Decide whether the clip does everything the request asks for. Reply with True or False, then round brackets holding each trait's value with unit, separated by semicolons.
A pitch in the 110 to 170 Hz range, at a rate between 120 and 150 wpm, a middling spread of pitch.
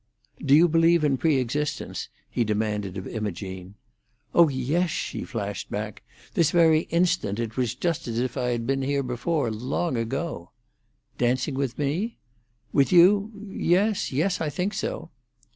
False (135 Hz; 145 wpm; 6.5 semitones)